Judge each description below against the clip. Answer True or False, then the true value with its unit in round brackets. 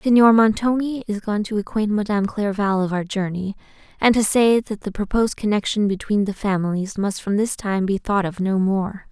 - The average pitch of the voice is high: True (205 Hz)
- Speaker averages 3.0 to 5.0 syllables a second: False (5.2 syllables/s)